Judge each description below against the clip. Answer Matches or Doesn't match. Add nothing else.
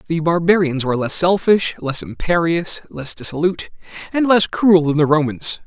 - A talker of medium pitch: Matches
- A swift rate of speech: Doesn't match